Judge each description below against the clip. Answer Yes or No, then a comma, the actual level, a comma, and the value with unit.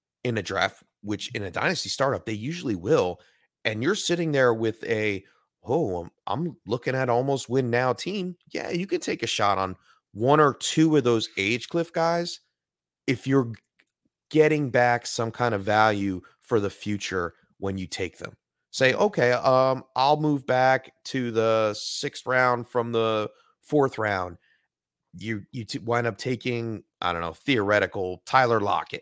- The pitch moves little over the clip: No, average, 4.2 semitones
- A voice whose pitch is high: No, low, 120 Hz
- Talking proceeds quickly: No, average, 170 wpm